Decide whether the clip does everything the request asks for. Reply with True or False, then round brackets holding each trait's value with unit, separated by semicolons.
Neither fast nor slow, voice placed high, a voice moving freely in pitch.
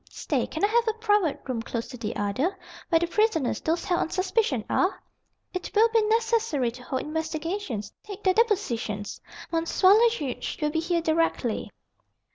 True (175 wpm; 335 Hz; 8.3 semitones)